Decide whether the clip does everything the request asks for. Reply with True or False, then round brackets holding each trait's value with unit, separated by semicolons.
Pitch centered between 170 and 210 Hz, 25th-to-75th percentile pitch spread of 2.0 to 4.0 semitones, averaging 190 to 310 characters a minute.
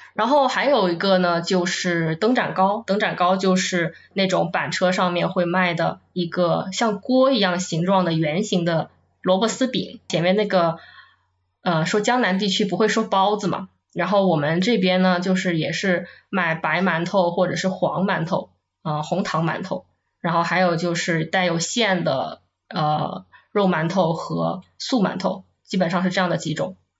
True (185 Hz; 2.4 semitones; 250 characters per minute)